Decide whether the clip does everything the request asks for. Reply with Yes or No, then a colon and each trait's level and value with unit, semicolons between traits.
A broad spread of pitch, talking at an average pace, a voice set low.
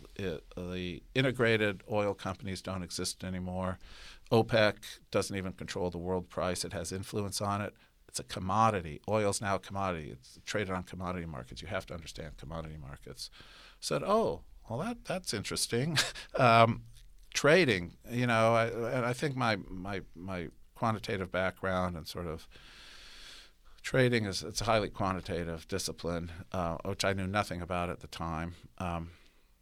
No: average, 3.5 semitones; average, 160 wpm; very low, 95 Hz